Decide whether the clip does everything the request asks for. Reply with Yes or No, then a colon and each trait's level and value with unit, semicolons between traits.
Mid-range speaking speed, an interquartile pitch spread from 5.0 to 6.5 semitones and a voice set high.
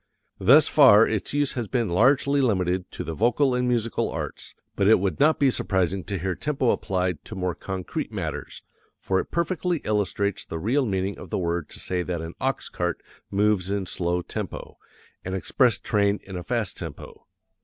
No: average, 185 wpm; wide, 5.4 semitones; low, 100 Hz